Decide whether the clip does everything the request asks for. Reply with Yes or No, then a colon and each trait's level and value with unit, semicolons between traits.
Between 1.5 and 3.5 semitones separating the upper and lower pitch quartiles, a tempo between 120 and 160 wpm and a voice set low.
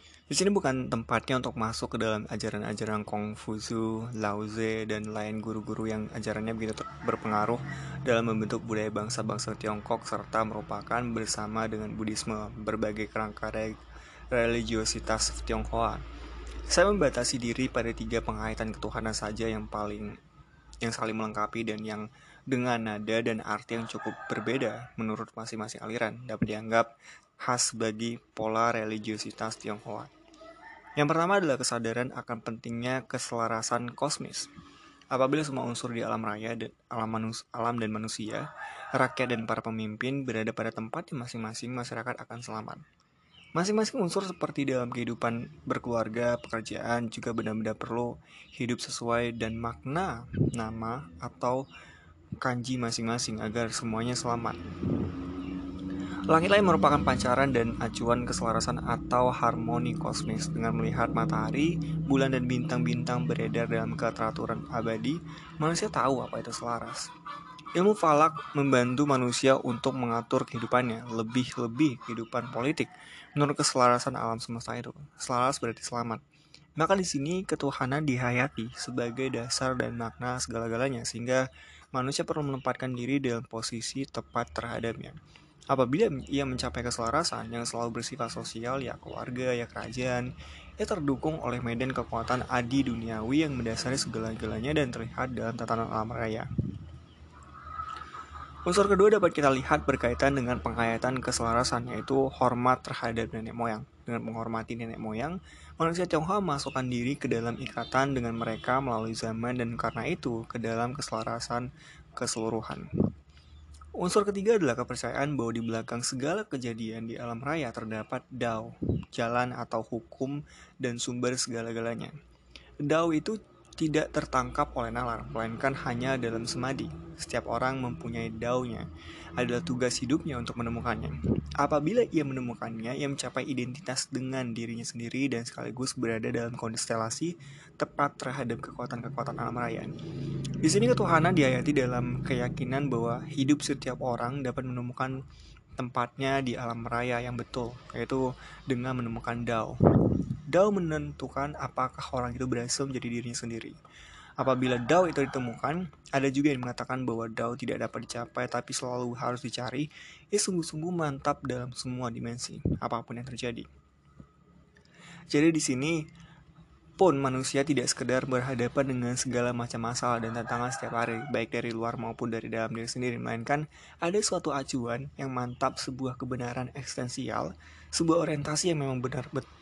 Yes: average, 2.9 semitones; average, 130 wpm; low, 120 Hz